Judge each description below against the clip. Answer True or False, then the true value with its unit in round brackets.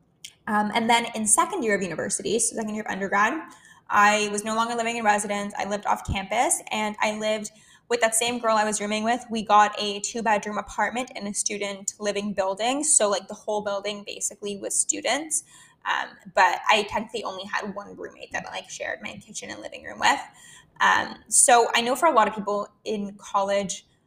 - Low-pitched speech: False (210 Hz)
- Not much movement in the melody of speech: True (2.1 semitones)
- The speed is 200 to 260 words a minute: True (205 wpm)